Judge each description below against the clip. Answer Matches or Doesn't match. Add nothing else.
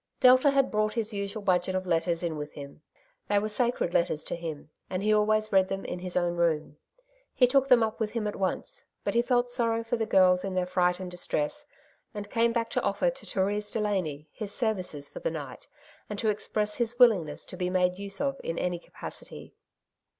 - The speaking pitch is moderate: Doesn't match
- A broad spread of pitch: Doesn't match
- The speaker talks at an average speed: Doesn't match